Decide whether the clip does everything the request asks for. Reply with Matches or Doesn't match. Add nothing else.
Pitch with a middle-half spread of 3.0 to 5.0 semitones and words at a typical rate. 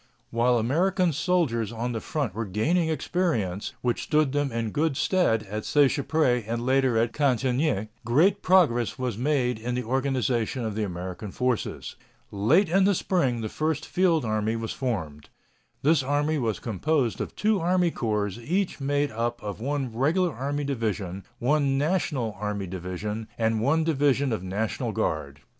Doesn't match